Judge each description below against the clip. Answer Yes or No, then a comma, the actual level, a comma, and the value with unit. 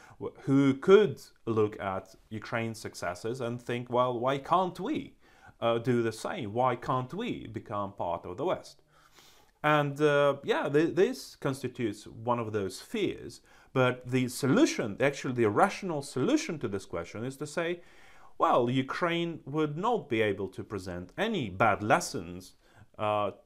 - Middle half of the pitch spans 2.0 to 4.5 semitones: No, average, 5.2 semitones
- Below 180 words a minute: Yes, average, 150 wpm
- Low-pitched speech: Yes, low, 125 Hz